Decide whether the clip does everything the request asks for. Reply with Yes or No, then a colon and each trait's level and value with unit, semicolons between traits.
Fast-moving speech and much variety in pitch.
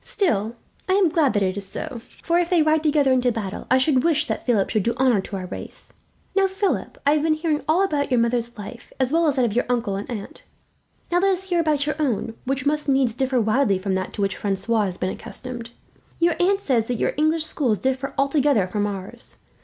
Yes: fast, 235 wpm; wide, 5.9 semitones